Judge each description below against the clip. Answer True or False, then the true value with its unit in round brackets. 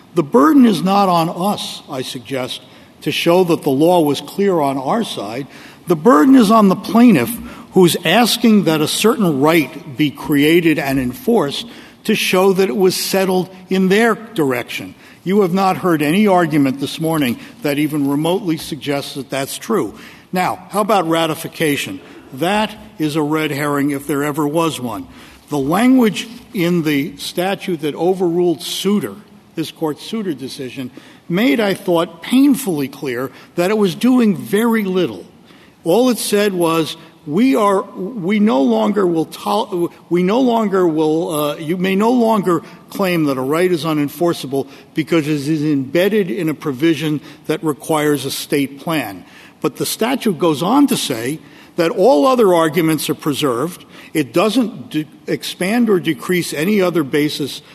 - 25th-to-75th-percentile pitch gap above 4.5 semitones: True (5.3 semitones)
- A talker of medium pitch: True (170 Hz)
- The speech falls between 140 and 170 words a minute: True (160 wpm)